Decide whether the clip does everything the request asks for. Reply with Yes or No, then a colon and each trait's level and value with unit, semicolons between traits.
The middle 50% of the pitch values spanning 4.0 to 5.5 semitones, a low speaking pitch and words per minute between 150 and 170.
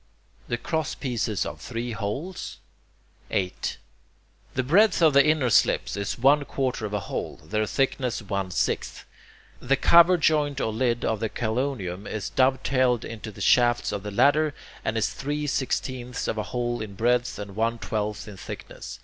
Yes: average, 4.3 semitones; low, 120 Hz; average, 165 wpm